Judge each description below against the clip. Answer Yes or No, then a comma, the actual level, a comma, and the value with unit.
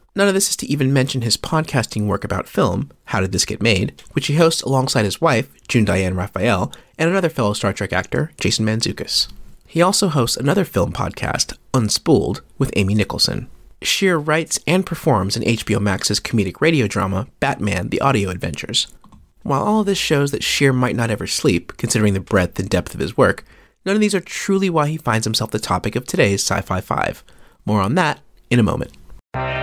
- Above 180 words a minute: Yes, average, 200 wpm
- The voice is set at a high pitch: No, low, 115 Hz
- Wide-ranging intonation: Yes, wide, 7.6 semitones